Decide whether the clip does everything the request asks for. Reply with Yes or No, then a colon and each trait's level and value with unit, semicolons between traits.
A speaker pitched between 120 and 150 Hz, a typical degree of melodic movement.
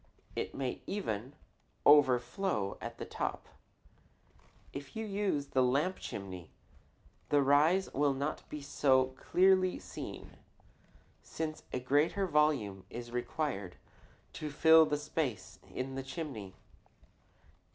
Yes: medium, 140 Hz; average, 4.3 semitones